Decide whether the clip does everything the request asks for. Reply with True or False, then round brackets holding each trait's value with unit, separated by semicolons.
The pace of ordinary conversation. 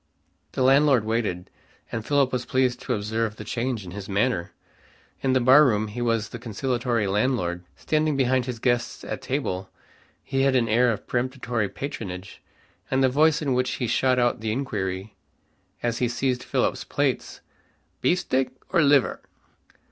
True (160 wpm)